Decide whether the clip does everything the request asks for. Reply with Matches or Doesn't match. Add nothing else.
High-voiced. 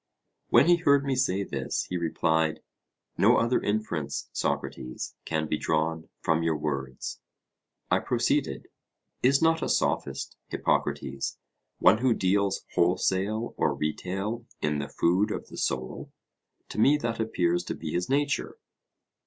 Doesn't match